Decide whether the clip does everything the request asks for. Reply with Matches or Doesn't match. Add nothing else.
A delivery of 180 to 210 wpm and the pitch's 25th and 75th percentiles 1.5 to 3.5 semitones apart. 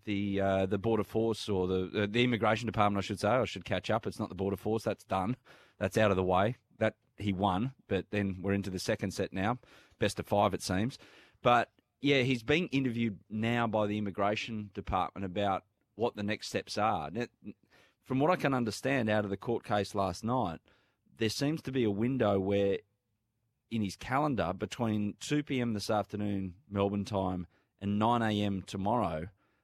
Matches